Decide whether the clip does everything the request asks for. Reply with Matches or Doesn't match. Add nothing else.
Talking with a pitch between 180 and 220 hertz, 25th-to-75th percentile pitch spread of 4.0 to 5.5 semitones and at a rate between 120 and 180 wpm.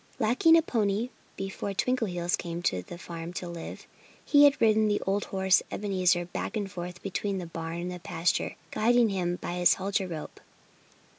Doesn't match